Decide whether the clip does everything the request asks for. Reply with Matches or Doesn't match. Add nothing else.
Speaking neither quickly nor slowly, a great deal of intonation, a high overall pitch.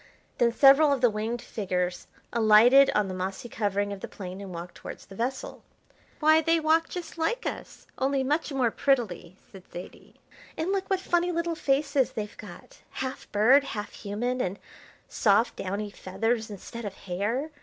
Matches